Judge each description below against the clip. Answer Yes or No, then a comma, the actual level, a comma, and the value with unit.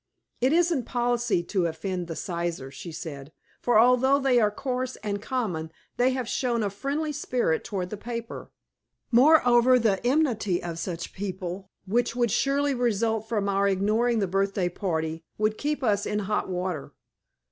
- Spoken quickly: No, average, 160 wpm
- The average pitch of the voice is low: No, high, 215 Hz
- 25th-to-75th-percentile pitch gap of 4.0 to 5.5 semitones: Yes, average, 5.1 semitones